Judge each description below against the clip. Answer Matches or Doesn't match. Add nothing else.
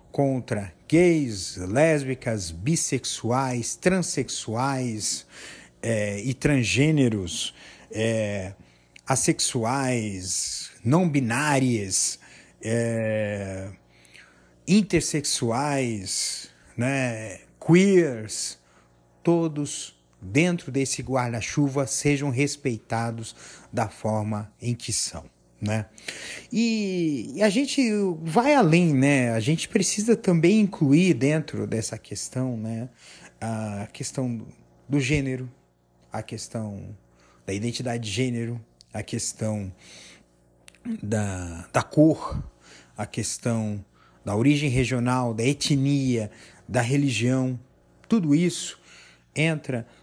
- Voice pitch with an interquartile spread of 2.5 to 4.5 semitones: Doesn't match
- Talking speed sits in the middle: Doesn't match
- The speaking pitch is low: Matches